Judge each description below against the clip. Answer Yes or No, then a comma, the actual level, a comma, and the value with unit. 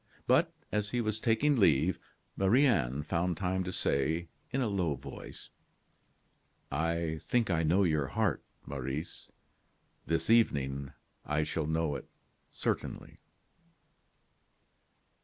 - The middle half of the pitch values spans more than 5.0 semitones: Yes, wide, 5.5 semitones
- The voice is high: No, very low, 85 Hz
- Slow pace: Yes, slow, 120 wpm